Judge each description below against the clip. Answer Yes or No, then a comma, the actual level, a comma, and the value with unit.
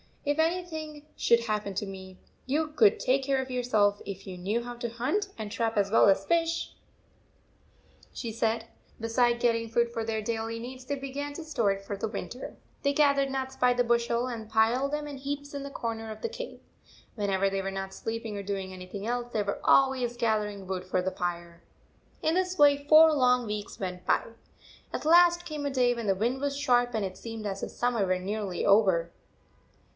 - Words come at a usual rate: No, fast, 210 wpm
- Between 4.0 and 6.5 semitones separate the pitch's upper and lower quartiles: Yes, average, 5.2 semitones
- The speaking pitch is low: No, high, 235 Hz